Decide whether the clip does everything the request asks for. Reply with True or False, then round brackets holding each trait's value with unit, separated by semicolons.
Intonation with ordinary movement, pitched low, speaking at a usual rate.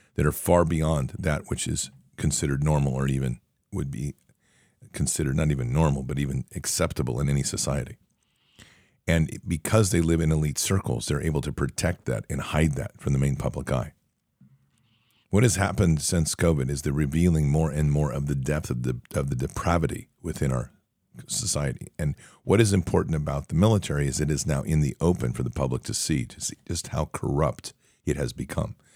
True (3.8 semitones; 75 Hz; 190 wpm)